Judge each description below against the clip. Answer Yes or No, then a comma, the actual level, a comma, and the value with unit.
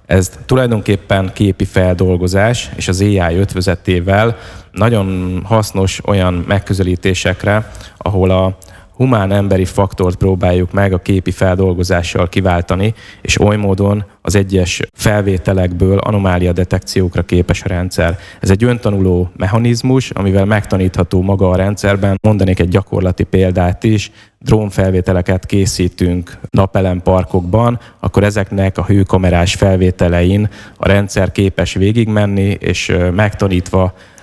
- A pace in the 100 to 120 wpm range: Yes, average, 110 wpm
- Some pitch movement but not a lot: No, narrow, 1.7 semitones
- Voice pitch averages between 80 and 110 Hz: Yes, very low, 95 Hz